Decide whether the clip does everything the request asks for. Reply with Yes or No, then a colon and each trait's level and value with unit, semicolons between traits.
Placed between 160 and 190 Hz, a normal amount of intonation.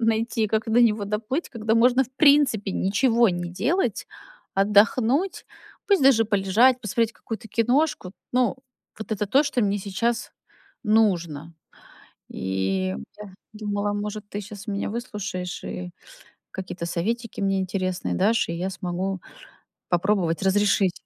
No: high, 210 Hz; average, 3.5 semitones